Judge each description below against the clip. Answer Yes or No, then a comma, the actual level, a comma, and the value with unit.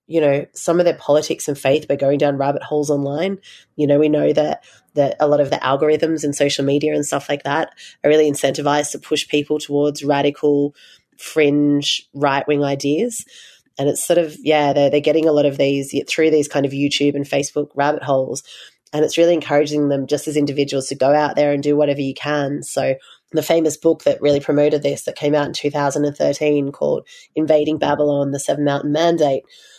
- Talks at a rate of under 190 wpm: No, fast, 205 wpm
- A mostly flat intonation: Yes, narrow, 1.2 semitones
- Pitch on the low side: No, medium, 145 Hz